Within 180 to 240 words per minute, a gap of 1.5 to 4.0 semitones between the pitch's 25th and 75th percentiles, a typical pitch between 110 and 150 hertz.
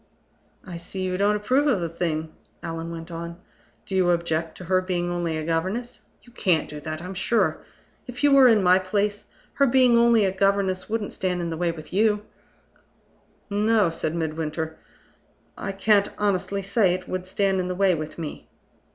No: average, 185 wpm; average, 3.6 semitones; medium, 185 Hz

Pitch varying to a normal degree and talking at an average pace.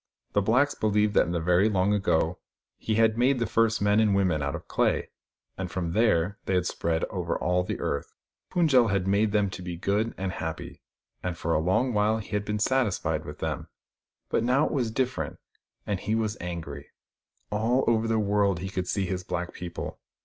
No: average, 3.9 semitones; fast, 210 wpm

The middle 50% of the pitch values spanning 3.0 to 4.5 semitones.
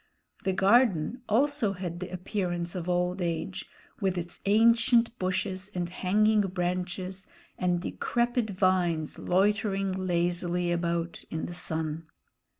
No: narrow, 2.5 semitones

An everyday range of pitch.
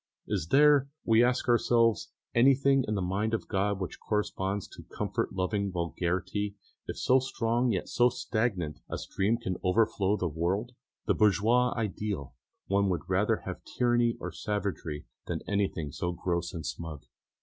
Yes: average, 4.3 semitones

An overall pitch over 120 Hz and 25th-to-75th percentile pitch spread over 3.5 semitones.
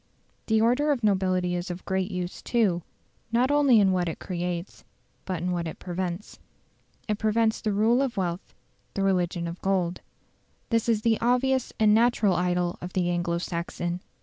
Yes: high, 190 Hz; average, 4.1 semitones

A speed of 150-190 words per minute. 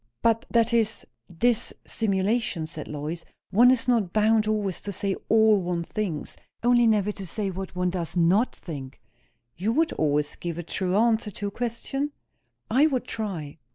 Yes: average, 165 wpm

